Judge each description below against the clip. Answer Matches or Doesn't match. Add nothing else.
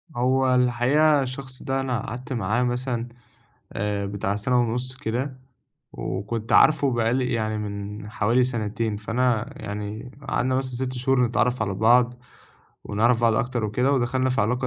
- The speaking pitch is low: Matches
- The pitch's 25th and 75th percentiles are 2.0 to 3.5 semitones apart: Matches